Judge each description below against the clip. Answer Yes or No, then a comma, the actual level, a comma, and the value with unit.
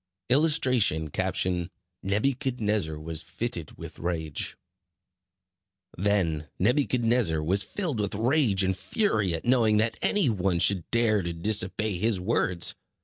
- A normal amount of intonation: No, wide, 5.8 semitones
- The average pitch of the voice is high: No, low, 105 Hz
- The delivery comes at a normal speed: No, slow, 115 wpm